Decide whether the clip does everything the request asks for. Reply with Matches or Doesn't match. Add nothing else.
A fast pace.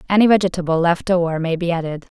Doesn't match